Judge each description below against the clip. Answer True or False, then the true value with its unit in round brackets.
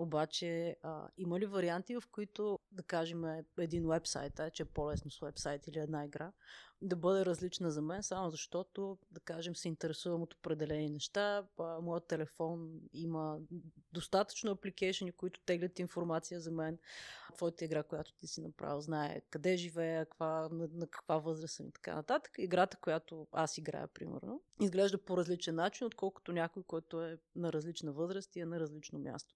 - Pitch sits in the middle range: True (170 Hz)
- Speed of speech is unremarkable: False (170 wpm)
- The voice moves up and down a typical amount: False (2.3 semitones)